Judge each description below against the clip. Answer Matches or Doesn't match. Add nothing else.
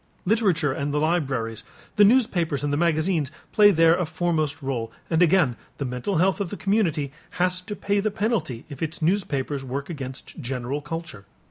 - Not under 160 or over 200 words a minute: Matches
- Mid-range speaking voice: Matches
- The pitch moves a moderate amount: Matches